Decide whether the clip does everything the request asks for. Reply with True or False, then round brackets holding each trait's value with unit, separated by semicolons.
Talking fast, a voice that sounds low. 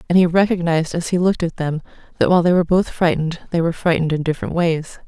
False (235 wpm; 170 Hz)